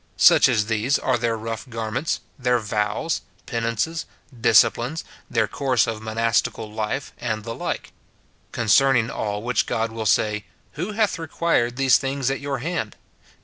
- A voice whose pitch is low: Yes, low, 115 Hz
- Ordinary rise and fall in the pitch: Yes, average, 3.6 semitones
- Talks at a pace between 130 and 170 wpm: Yes, average, 150 wpm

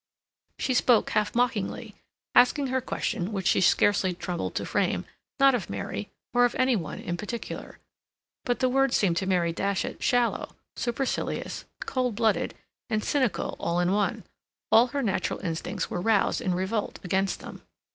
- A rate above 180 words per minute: No, average, 160 wpm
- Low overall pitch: No, high, 210 Hz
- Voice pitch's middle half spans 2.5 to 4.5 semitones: No, average, 5.1 semitones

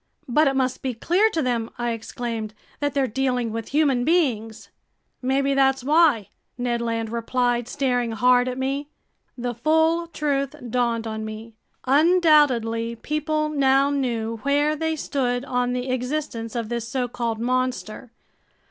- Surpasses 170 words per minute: No, average, 150 wpm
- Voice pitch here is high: Yes, very high, 250 Hz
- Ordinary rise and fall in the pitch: Yes, average, 3.4 semitones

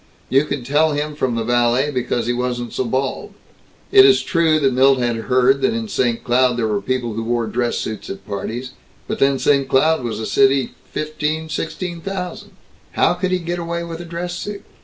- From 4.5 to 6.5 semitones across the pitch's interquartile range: Yes, average, 5.2 semitones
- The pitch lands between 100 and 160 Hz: Yes, low, 135 Hz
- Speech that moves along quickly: Yes, fast, 210 wpm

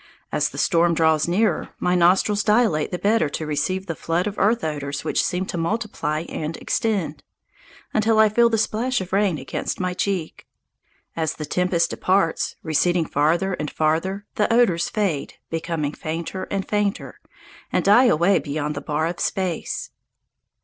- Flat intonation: No, average, 4.4 semitones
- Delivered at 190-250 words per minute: No, average, 165 wpm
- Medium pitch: Yes, medium, 180 Hz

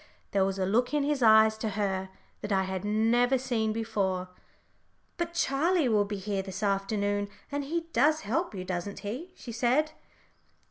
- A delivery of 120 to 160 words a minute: No, average, 175 wpm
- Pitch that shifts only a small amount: No, average, 5.2 semitones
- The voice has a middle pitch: No, high, 220 Hz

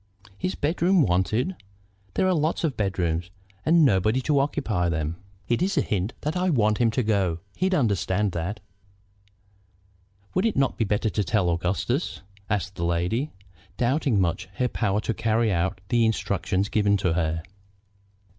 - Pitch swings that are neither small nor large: No, wide, 6.9 semitones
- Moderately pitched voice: No, low, 105 Hz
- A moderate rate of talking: Yes, average, 155 wpm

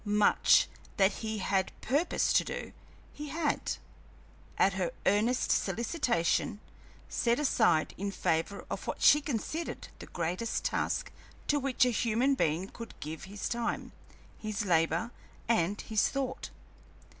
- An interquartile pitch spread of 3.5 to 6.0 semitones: Yes, average, 4.8 semitones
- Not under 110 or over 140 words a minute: Yes, slow, 135 wpm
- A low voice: No, high, 220 Hz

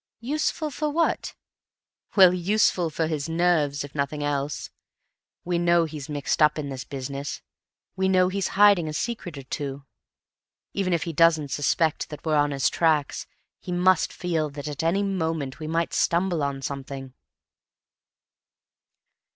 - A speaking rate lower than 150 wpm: No, average, 155 wpm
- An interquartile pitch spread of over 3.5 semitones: Yes, average, 3.9 semitones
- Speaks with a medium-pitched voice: Yes, medium, 160 Hz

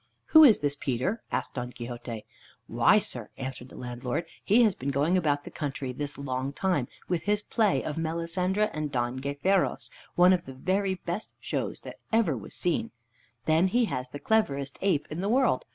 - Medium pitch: Yes, medium, 155 Hz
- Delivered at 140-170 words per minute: No, average, 185 wpm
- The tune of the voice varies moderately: No, wide, 6.2 semitones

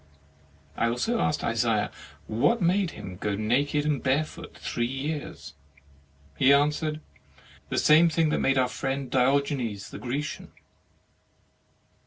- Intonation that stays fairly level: No, average, 4.0 semitones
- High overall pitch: No, medium, 140 Hz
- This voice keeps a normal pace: No, slow, 120 wpm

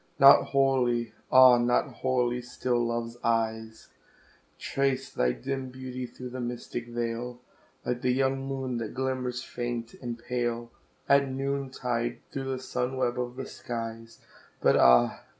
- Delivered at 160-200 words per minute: No, average, 140 wpm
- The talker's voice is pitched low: Yes, low, 125 Hz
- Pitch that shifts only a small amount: Yes, narrow, 1.7 semitones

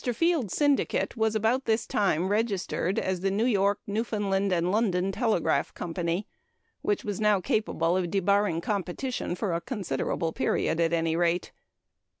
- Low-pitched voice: No, high, 195 Hz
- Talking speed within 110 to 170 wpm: Yes, average, 150 wpm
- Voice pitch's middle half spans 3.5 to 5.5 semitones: Yes, average, 3.8 semitones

